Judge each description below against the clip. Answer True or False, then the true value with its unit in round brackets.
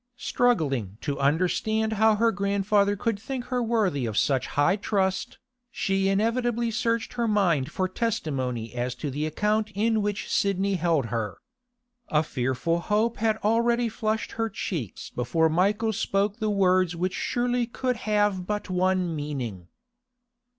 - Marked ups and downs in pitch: True (5.9 semitones)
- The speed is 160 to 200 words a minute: False (145 wpm)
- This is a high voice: True (200 Hz)